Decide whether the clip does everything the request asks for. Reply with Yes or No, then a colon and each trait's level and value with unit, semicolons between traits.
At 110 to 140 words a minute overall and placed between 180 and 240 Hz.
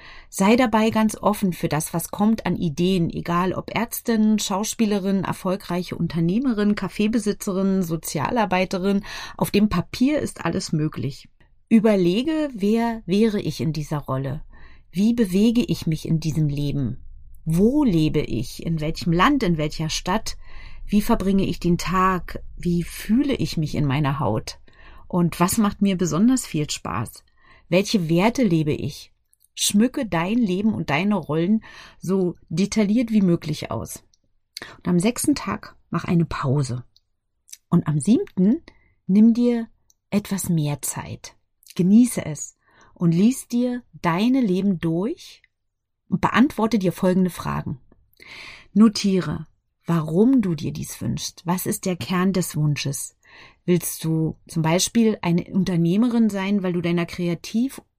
Yes: average, 135 wpm; medium, 185 Hz